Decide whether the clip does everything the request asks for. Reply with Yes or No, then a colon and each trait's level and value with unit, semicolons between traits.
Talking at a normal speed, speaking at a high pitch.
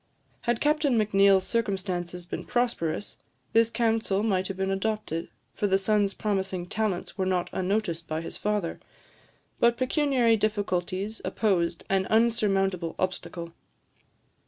No: slow, 125 wpm; high, 195 Hz